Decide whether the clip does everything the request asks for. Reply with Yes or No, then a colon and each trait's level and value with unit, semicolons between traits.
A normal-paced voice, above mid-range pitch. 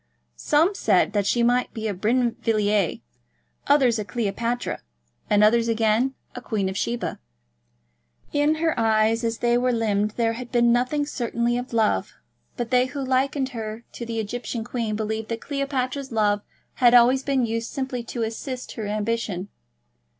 Yes: average, 160 wpm; high, 235 Hz